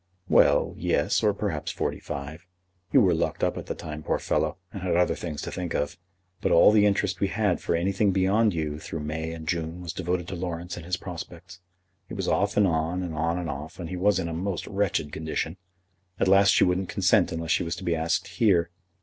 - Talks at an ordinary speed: No, fast, 225 wpm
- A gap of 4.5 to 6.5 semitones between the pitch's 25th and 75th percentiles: No, average, 2.9 semitones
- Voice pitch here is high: No, very low, 85 Hz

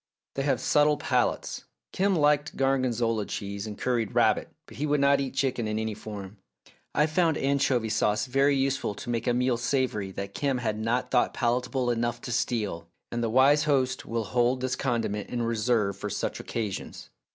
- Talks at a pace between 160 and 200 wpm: Yes, average, 185 wpm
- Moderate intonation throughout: Yes, average, 3.7 semitones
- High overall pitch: No, low, 120 Hz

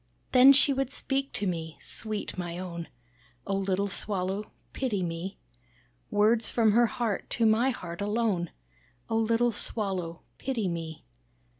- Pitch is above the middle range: Yes, high, 205 Hz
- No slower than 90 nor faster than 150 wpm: Yes, average, 140 wpm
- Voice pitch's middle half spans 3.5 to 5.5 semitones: Yes, average, 4.4 semitones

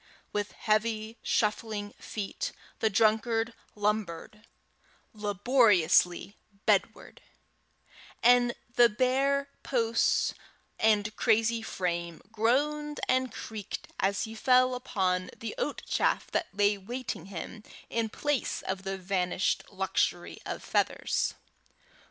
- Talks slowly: Yes, slow, 105 wpm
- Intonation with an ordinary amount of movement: Yes, average, 3.2 semitones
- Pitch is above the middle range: Yes, high, 220 Hz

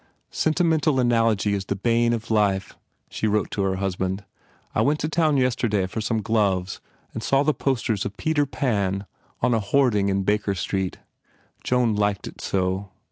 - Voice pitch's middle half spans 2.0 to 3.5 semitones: No, average, 4.3 semitones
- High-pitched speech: No, low, 105 Hz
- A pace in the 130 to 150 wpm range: No, average, 175 wpm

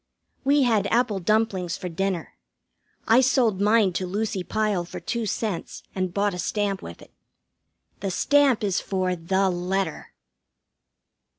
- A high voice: Yes, high, 195 Hz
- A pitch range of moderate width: Yes, average, 3.2 semitones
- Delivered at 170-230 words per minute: No, average, 140 wpm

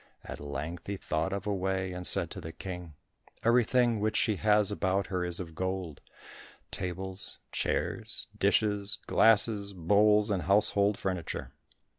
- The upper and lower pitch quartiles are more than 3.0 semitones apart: No, narrow, 2.6 semitones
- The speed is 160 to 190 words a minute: No, average, 140 wpm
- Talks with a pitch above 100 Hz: No, very low, 95 Hz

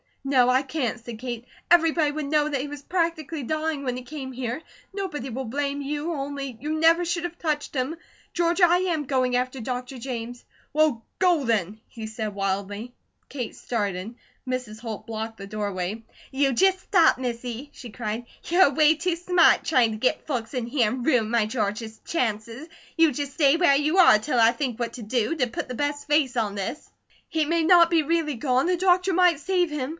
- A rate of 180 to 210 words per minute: Yes, average, 200 wpm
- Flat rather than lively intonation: No, average, 5.2 semitones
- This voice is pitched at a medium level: No, very high, 270 Hz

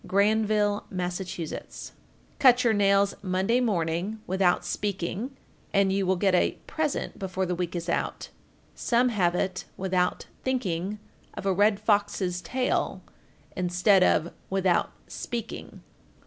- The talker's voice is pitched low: No, high, 195 Hz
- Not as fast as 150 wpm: Yes, slow, 135 wpm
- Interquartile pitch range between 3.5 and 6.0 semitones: No, average, 2.9 semitones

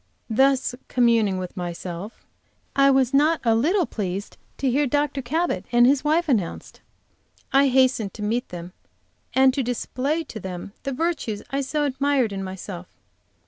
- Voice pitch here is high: Yes, very high, 255 Hz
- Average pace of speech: Yes, average, 155 wpm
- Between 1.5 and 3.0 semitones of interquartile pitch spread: No, wide, 5.4 semitones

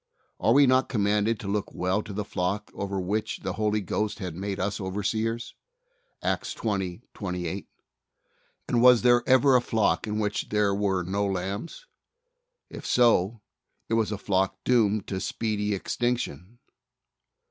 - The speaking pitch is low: Yes, low, 105 Hz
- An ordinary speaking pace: Yes, average, 150 wpm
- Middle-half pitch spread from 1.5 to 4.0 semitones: Yes, average, 2.7 semitones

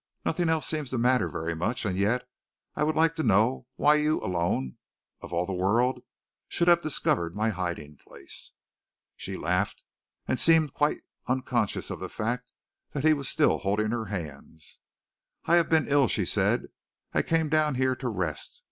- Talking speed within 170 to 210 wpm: Yes, average, 175 wpm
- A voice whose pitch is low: Yes, low, 125 Hz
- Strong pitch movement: Yes, wide, 8.2 semitones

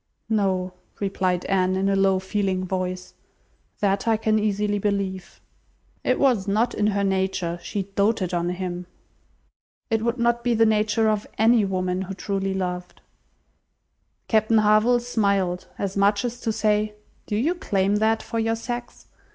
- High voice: Yes, high, 200 Hz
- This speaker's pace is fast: No, average, 155 wpm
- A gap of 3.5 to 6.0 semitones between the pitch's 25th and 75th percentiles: No, average, 2.7 semitones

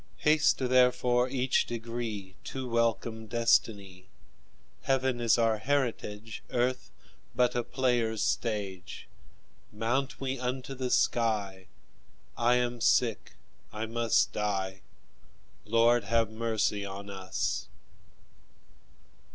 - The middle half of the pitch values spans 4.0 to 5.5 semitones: No, average, 3.0 semitones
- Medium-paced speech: No, slow, 100 wpm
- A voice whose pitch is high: No, low, 115 Hz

